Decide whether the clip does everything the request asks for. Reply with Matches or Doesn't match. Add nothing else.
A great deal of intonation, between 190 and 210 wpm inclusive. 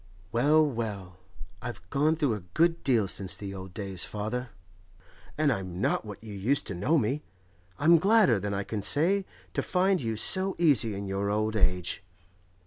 Doesn't match